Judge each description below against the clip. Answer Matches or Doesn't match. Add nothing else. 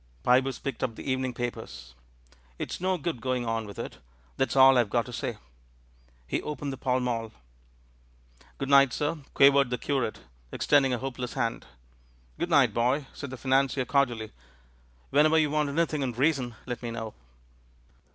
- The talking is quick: Doesn't match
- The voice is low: Matches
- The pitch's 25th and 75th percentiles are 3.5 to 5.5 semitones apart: Doesn't match